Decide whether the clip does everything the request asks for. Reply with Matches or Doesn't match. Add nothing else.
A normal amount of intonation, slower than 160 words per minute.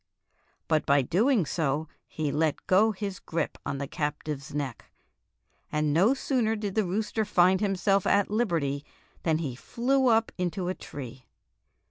Doesn't match